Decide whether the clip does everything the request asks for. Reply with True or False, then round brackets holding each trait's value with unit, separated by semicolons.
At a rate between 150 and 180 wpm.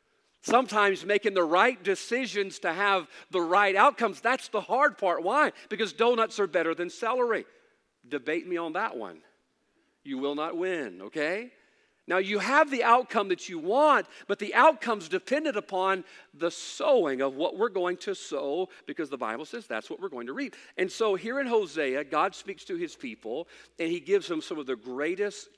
False (190 wpm)